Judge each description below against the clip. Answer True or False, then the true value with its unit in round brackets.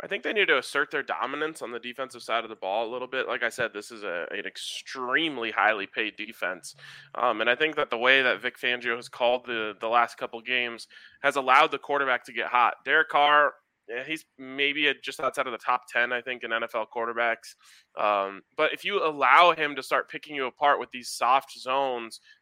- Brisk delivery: True (225 wpm)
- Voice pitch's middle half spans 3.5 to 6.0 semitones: False (2.8 semitones)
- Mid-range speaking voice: False (125 Hz)